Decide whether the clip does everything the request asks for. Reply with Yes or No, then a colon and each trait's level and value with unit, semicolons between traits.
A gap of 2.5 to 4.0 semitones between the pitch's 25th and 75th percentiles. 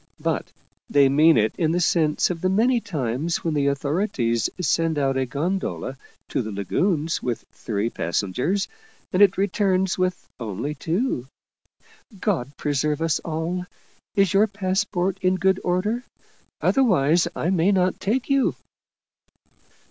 No: wide, 5.4 semitones